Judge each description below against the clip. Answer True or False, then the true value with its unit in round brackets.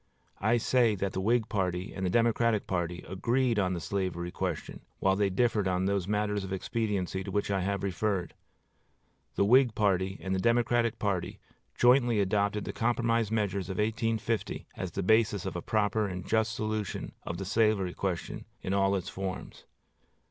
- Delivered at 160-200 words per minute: True (175 wpm)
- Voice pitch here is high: False (100 Hz)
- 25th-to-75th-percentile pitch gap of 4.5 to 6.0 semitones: False (2.9 semitones)